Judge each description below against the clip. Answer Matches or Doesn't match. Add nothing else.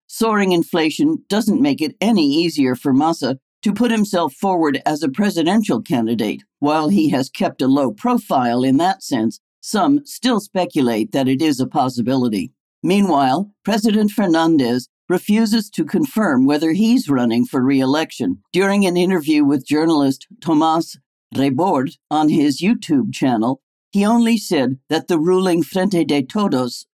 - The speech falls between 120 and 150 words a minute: Matches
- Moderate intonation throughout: Doesn't match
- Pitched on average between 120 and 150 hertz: Doesn't match